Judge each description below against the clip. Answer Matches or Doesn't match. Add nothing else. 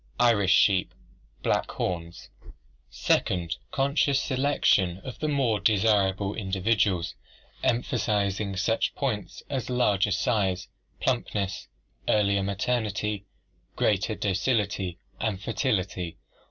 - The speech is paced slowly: Matches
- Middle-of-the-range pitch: Doesn't match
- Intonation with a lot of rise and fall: Doesn't match